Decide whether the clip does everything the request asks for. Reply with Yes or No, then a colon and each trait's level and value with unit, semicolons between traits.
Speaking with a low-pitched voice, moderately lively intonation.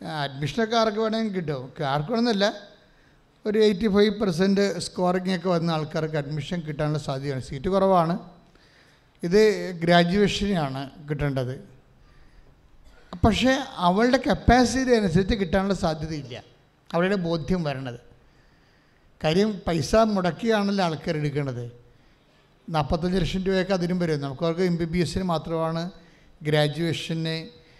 No: medium, 170 Hz; average, 4.7 semitones